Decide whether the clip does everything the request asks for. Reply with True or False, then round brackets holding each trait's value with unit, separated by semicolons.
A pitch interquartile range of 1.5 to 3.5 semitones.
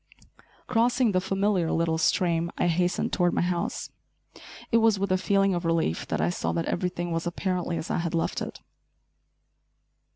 True (2.8 semitones)